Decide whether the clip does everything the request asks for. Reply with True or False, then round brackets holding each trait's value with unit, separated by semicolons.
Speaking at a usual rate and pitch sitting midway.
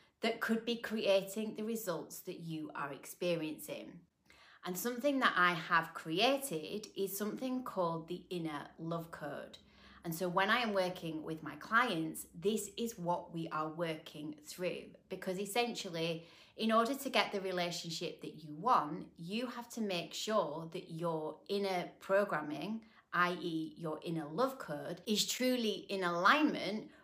True (150 wpm; 180 Hz)